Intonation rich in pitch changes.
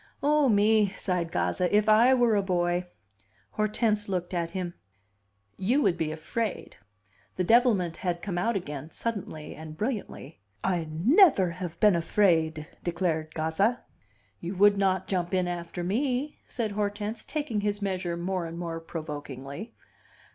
No: average, 3.9 semitones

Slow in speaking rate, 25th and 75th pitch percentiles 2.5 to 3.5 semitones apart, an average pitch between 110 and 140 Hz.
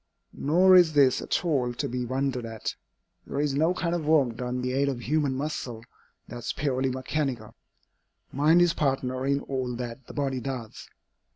No: average, 185 wpm; average, 3.1 semitones; low, 135 Hz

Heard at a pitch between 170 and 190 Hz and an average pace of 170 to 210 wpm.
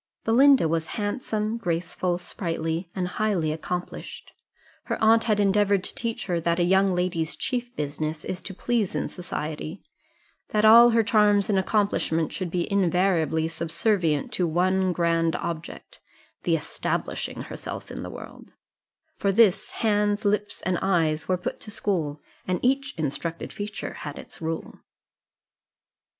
No: medium, 185 Hz; average, 145 wpm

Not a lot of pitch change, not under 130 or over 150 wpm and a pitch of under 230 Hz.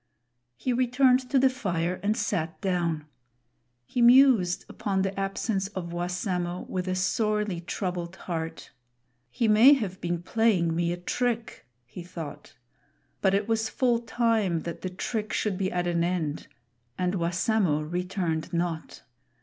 No: average, 4.2 semitones; average, 145 wpm; medium, 185 Hz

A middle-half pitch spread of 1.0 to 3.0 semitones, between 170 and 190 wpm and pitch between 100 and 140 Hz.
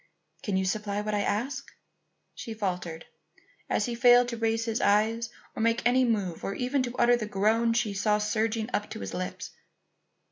No: narrow, 2.4 semitones; average, 185 wpm; high, 220 Hz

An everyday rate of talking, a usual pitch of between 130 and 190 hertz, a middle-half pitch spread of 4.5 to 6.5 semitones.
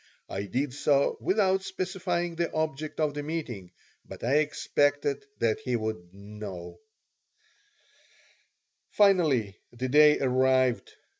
No: slow, 115 wpm; medium, 140 Hz; average, 5.2 semitones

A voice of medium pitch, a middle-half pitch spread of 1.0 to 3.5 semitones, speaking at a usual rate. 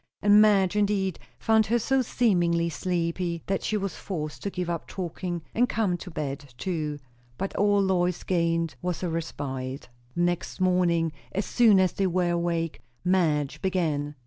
Yes: medium, 180 Hz; average, 2.8 semitones; average, 170 wpm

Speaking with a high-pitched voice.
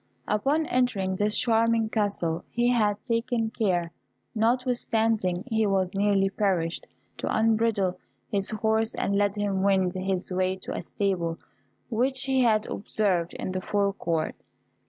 Yes: high, 205 Hz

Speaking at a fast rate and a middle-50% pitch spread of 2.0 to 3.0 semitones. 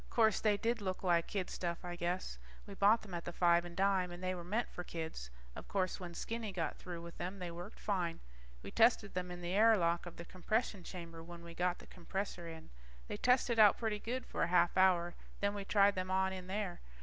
Yes: fast, 235 wpm; average, 2.7 semitones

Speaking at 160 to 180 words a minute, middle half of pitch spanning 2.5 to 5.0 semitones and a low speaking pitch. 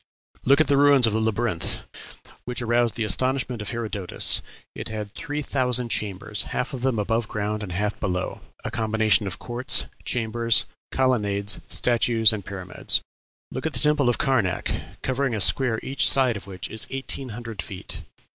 Yes: average, 170 wpm; average, 3.5 semitones; low, 115 Hz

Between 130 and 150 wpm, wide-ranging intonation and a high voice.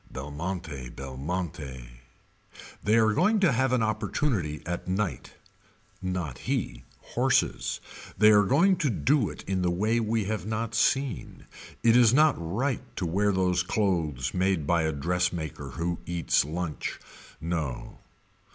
No: average, 140 wpm; wide, 5.8 semitones; very low, 90 Hz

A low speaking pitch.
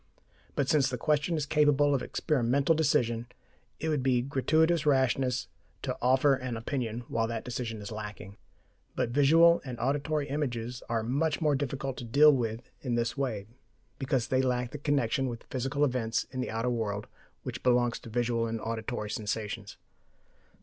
Yes: low, 125 Hz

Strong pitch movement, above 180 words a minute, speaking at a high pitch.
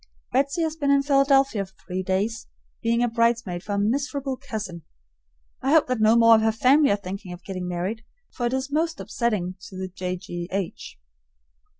Yes: wide, 6.2 semitones; average, 190 wpm; high, 225 Hz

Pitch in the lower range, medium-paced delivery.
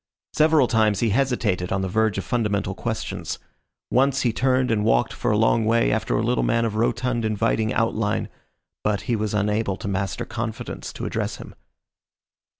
Yes: low, 110 Hz; average, 175 wpm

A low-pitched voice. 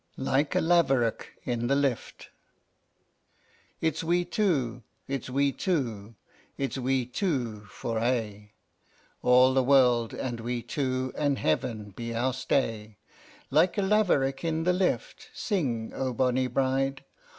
Yes: low, 130 Hz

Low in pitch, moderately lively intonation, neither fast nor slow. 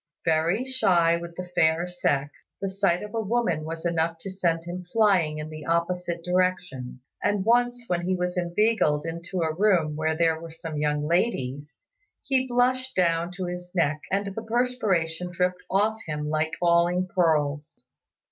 No: medium, 175 Hz; average, 3.2 semitones; average, 165 wpm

